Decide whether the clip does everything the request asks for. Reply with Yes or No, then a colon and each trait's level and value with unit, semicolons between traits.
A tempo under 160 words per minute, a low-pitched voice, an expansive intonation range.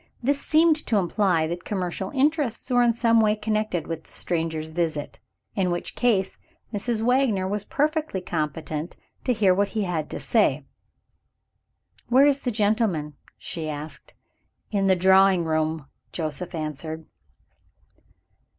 No: average, 140 wpm; high, 190 Hz; wide, 6.1 semitones